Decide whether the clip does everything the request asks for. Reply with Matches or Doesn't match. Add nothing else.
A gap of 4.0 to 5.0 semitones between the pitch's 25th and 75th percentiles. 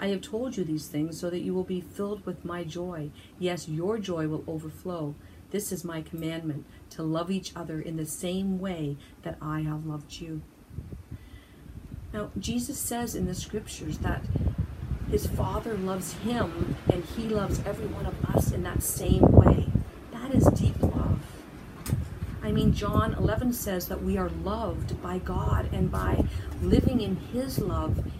Doesn't match